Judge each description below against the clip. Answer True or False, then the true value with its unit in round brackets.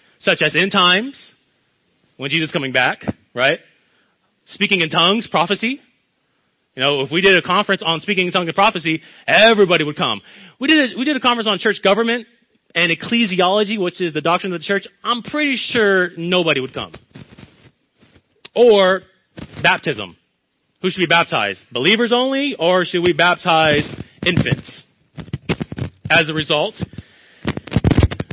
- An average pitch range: True (4.7 semitones)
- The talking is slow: False (150 wpm)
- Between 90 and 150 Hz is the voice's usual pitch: False (185 Hz)